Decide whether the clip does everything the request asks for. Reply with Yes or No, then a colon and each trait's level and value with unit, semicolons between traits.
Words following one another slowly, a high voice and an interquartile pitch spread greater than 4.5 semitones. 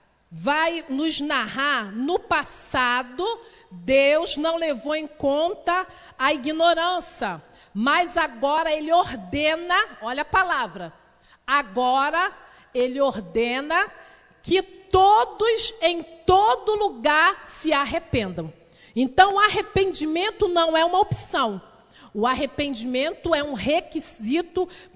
Yes: slow, 100 wpm; very high, 315 Hz; average, 5.1 semitones